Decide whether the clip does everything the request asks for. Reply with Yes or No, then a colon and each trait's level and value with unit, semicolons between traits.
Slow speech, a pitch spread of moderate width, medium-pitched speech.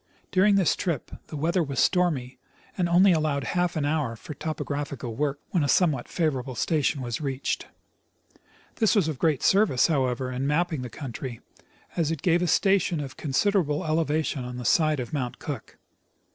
No: average, 175 wpm; average, 4.5 semitones; medium, 150 Hz